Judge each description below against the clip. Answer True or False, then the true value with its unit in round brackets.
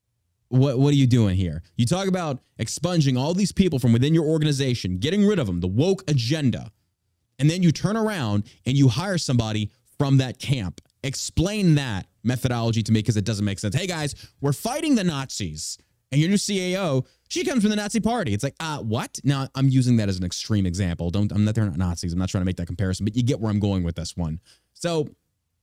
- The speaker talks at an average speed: False (230 wpm)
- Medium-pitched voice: False (125 Hz)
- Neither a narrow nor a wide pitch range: False (6.7 semitones)